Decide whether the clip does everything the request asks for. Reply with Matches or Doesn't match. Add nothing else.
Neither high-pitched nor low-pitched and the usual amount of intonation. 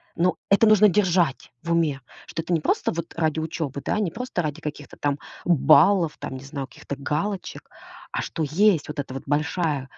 Matches